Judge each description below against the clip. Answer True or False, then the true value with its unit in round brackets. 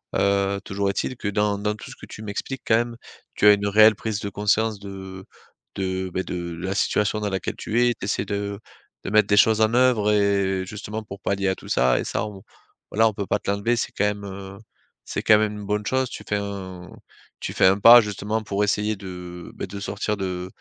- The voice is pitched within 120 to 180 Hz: False (100 Hz)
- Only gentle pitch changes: True (1.6 semitones)